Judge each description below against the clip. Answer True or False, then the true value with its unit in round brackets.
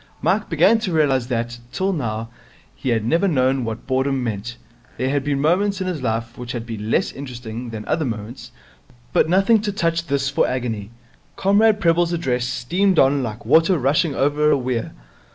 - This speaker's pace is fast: False (185 wpm)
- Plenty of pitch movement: True (6.0 semitones)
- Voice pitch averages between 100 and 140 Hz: True (135 Hz)